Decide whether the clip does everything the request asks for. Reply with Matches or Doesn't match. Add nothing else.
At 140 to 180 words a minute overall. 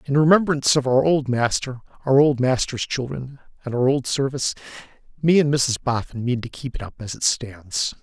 Doesn't match